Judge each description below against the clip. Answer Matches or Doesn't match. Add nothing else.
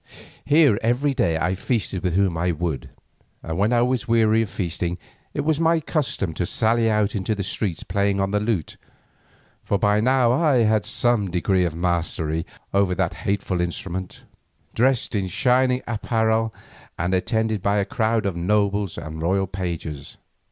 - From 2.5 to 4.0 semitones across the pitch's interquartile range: Doesn't match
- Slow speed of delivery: Doesn't match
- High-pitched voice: Doesn't match